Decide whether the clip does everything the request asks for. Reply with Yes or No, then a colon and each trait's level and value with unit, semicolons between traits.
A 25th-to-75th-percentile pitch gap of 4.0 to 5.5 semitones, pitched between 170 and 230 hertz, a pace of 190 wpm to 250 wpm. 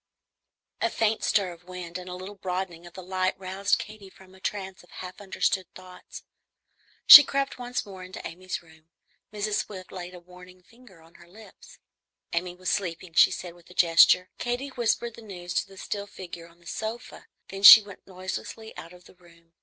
No: narrow, 2.4 semitones; medium, 185 Hz; average, 195 wpm